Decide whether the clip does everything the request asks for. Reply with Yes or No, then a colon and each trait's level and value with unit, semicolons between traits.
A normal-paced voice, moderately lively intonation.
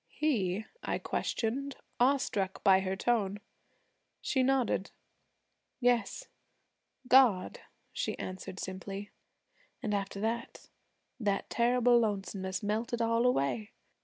No: slow, 100 wpm; average, 4.1 semitones